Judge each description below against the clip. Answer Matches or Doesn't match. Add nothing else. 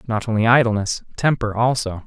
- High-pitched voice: Doesn't match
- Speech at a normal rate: Matches